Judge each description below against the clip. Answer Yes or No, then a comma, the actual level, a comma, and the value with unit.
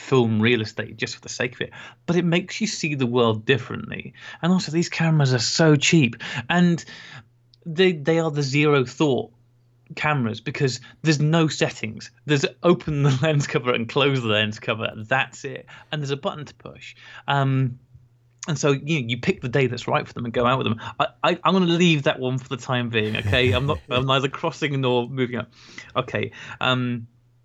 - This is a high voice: No, low, 130 Hz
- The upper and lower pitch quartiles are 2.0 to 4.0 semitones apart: No, average, 4.4 semitones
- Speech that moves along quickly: Yes, fast, 210 wpm